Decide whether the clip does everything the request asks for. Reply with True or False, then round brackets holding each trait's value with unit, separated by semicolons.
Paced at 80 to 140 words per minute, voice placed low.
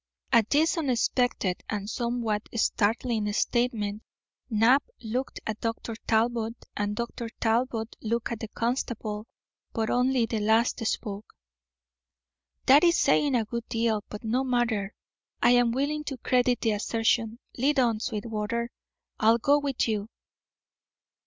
False (135 wpm; 230 Hz)